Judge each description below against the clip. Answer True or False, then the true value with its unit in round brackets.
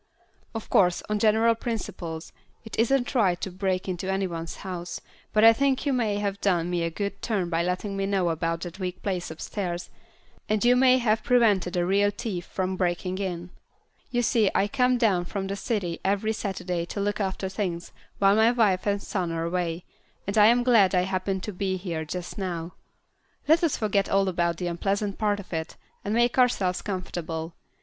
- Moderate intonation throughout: True (3.3 semitones)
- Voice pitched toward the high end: True (195 Hz)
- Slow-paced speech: False (195 wpm)